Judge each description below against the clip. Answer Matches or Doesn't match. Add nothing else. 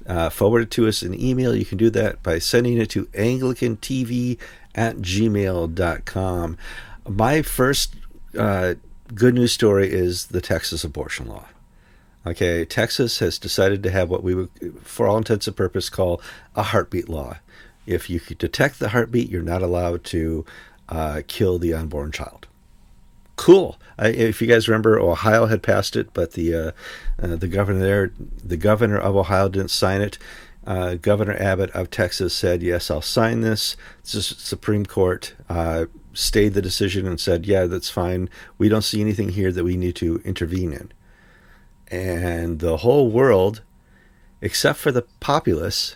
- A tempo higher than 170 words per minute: Doesn't match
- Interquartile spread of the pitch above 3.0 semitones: Matches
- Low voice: Matches